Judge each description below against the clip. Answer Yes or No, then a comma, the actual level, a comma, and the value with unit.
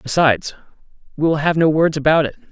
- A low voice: No, medium, 155 Hz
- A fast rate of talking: No, average, 190 wpm